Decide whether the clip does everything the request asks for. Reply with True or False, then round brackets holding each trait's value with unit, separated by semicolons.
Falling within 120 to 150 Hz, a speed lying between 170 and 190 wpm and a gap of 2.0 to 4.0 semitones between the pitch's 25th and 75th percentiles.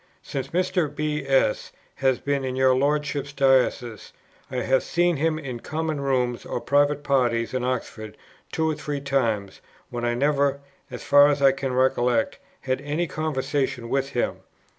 False (135 Hz; 160 wpm; 2.4 semitones)